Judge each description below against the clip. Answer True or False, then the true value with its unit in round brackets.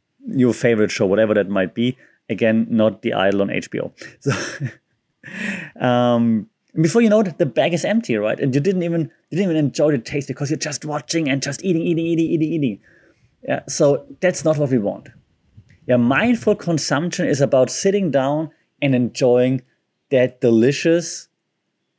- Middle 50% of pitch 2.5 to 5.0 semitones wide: False (5.6 semitones)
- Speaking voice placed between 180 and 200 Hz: False (140 Hz)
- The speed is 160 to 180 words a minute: True (175 wpm)